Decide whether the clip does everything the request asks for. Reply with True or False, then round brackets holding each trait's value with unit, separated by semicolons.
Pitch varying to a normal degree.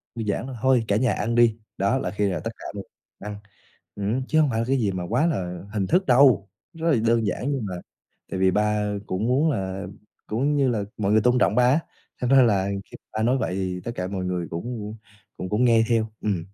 True (4.2 semitones)